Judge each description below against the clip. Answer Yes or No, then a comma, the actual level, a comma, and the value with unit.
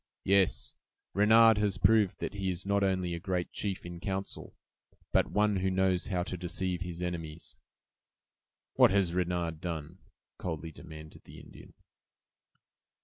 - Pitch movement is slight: Yes, narrow, 2.3 semitones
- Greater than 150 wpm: No, average, 145 wpm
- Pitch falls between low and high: No, very low, 90 Hz